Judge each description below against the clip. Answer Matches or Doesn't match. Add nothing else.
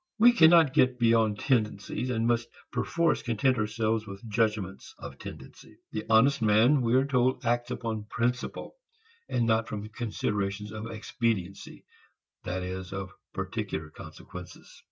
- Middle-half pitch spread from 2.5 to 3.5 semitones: Matches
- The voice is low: Matches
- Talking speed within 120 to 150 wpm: Matches